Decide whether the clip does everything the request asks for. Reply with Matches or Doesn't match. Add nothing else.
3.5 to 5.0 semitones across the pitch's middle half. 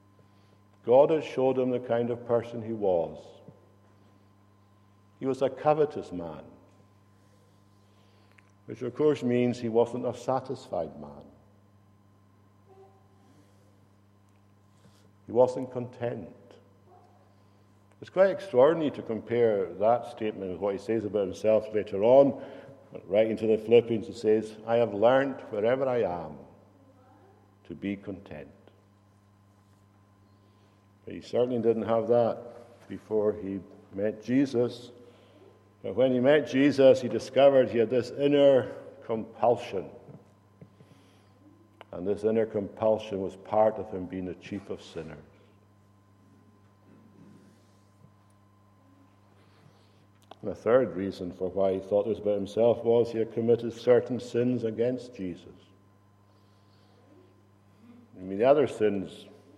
Doesn't match